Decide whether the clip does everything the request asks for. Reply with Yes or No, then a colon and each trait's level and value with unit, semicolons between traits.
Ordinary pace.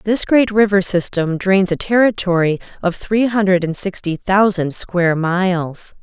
Yes: average, 150 wpm